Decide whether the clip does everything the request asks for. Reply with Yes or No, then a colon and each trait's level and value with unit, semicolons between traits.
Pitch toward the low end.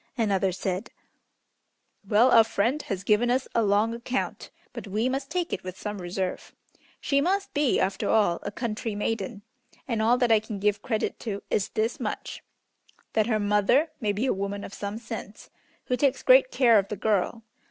No: high, 220 Hz